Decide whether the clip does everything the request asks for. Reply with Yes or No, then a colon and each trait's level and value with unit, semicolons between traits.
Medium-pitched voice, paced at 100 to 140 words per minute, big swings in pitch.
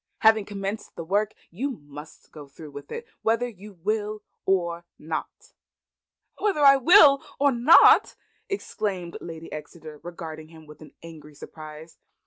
Yes: medium, 180 Hz; slow, 135 wpm; wide, 5.9 semitones